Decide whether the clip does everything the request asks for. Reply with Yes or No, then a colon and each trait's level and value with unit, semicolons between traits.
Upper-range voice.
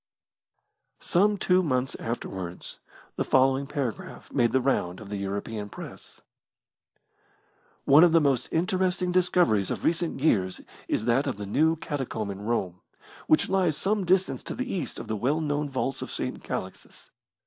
No: low, 135 Hz